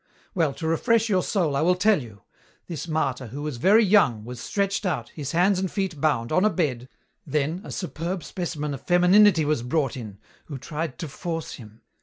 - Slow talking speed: No, average, 200 wpm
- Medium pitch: Yes, medium, 160 Hz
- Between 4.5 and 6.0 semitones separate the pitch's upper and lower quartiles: Yes, average, 5.2 semitones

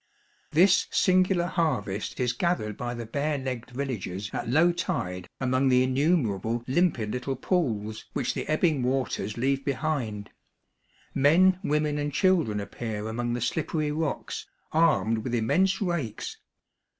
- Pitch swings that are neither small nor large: No, wide, 5.9 semitones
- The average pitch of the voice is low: Yes, low, 130 Hz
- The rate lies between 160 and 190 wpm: No, average, 140 wpm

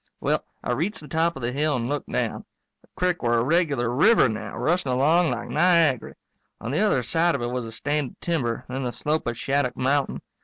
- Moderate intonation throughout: Yes, average, 5.0 semitones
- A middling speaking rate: No, fast, 225 wpm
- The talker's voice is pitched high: No, medium, 140 Hz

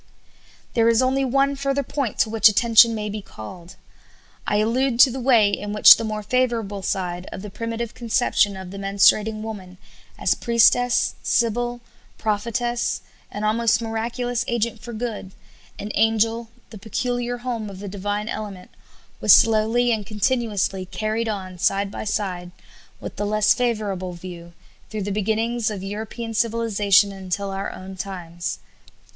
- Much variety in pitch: No, average, 2.9 semitones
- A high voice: Yes, high, 215 Hz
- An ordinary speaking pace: Yes, average, 150 wpm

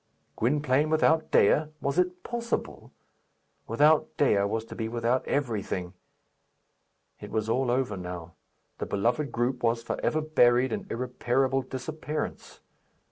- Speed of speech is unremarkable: No, slow, 130 wpm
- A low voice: Yes, low, 130 Hz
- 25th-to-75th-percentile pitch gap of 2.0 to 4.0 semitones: No, average, 4.8 semitones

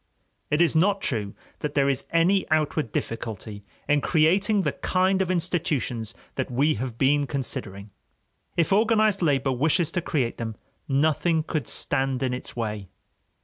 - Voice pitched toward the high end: No, medium, 145 Hz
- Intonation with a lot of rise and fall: Yes, wide, 5.7 semitones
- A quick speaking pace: No, average, 150 wpm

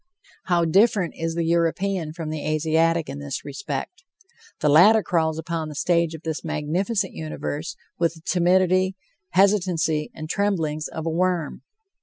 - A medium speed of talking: Yes, average, 150 wpm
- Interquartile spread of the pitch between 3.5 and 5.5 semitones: No, average, 2.8 semitones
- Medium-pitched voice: Yes, medium, 165 Hz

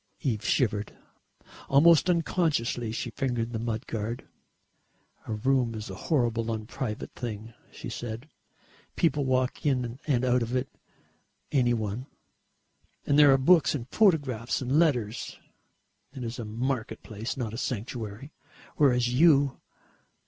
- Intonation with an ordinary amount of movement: Yes, average, 3.2 semitones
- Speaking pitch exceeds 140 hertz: No, low, 125 Hz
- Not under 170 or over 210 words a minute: No, slow, 135 wpm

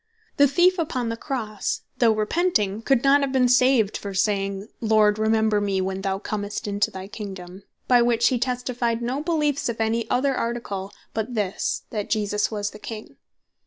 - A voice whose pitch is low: No, high, 220 Hz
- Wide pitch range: No, average, 3.5 semitones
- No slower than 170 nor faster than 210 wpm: Yes, average, 175 wpm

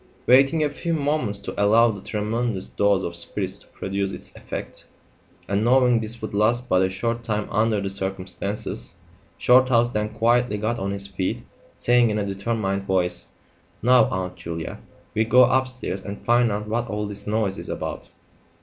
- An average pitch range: Yes, average, 3.3 semitones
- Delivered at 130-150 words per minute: No, average, 175 wpm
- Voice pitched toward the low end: Yes, low, 105 Hz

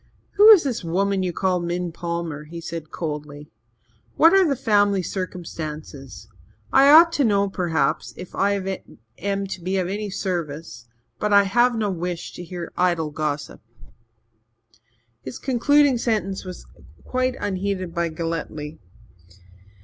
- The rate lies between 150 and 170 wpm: No, average, 140 wpm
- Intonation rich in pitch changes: No, average, 3.8 semitones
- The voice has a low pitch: No, medium, 185 Hz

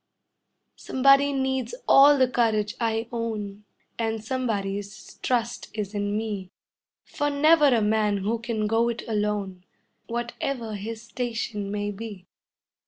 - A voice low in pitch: No, high, 225 Hz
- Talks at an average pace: No, slow, 130 wpm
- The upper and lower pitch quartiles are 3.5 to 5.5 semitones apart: No, average, 2.9 semitones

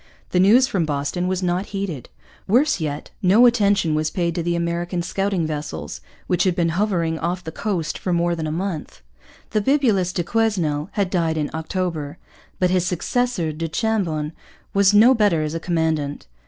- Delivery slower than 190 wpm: Yes, average, 180 wpm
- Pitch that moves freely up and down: No, average, 3.7 semitones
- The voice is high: No, medium, 175 Hz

